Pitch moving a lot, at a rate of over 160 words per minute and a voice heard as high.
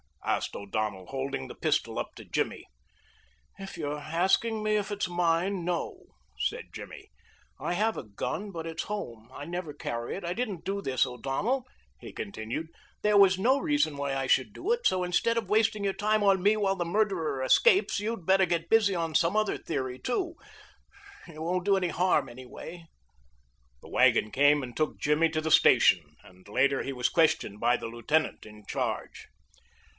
No: wide, 6.7 semitones; average, 180 wpm; medium, 170 Hz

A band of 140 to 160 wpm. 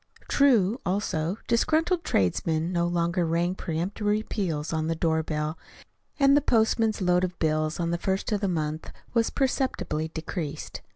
Yes: average, 150 wpm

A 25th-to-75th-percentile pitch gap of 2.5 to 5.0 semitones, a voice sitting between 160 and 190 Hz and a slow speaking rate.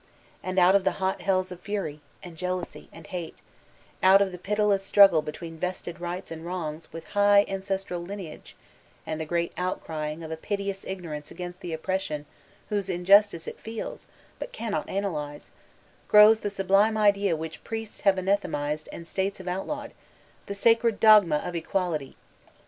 No: average, 3.4 semitones; medium, 185 Hz; average, 160 wpm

